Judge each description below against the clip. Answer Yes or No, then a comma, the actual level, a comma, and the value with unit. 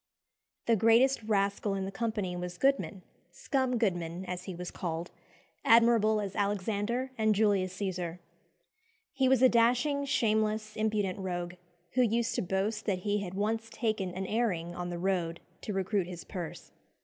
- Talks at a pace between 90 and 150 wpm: No, average, 160 wpm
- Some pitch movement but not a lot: Yes, average, 3.7 semitones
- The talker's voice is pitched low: No, high, 205 Hz